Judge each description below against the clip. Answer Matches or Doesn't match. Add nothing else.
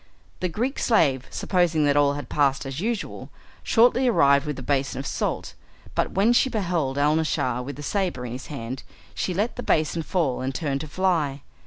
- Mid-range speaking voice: Matches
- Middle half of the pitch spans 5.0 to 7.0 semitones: Matches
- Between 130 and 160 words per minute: Doesn't match